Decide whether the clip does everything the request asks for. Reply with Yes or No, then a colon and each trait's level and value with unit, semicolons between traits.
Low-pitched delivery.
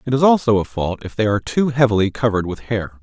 Yes: low, 115 Hz